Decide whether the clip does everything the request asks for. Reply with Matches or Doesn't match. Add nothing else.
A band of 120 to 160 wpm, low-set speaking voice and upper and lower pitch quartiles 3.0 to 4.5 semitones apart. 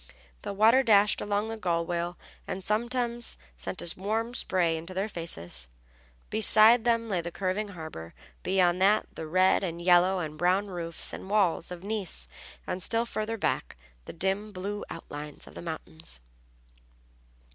Doesn't match